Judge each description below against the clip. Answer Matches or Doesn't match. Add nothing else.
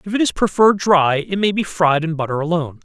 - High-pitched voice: Doesn't match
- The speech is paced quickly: Matches